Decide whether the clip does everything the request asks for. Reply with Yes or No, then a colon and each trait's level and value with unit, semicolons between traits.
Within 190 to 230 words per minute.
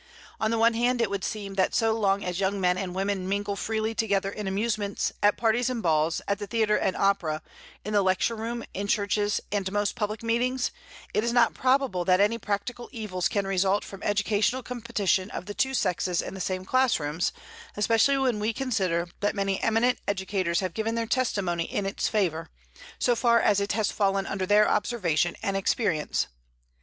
Yes: average, 195 wpm